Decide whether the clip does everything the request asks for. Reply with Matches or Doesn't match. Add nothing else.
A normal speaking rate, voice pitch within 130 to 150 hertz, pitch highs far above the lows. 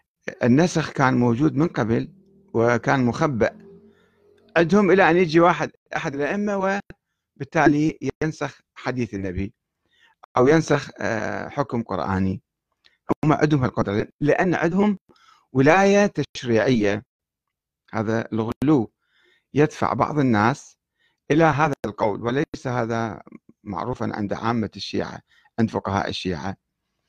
Matches